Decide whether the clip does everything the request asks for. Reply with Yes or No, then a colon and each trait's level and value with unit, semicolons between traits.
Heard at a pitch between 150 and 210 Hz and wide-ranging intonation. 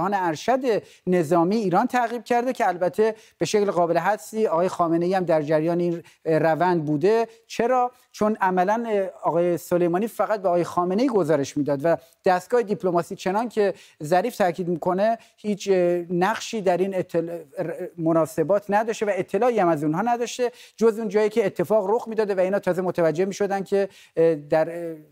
No: medium, 185 Hz; average, 4.2 semitones